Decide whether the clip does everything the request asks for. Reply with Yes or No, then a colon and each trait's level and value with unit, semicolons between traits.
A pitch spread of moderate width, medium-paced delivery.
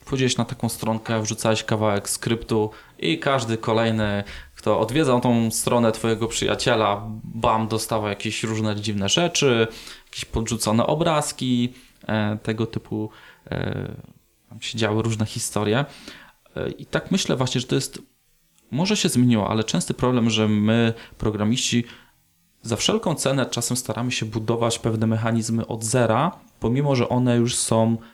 No: narrow, 2.1 semitones; average, 135 wpm